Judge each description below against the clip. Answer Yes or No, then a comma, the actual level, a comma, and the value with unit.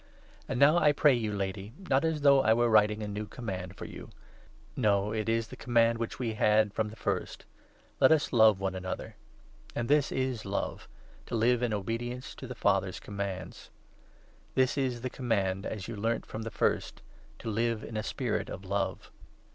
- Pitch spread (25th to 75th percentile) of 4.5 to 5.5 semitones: No, average, 3.4 semitones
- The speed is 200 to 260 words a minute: Yes, fast, 205 wpm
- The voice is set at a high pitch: No, low, 115 Hz